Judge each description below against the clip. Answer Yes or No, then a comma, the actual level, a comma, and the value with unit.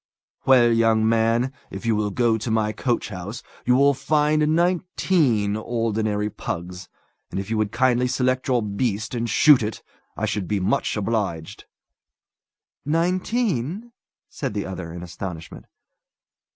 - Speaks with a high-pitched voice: No, low, 115 Hz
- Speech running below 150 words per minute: Yes, average, 140 wpm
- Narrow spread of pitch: No, average, 4.2 semitones